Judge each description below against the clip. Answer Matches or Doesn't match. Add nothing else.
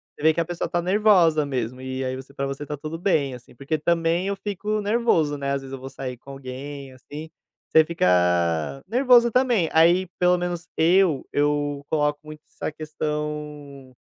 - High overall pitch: Doesn't match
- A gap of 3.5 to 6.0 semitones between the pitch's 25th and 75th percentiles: Matches